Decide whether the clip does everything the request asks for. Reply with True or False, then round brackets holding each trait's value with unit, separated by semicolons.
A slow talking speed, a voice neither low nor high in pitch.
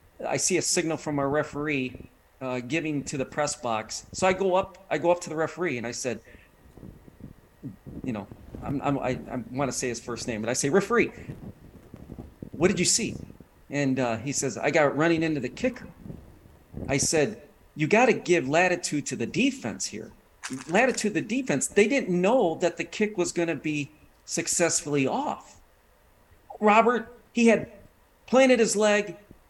False (175 wpm; 150 Hz)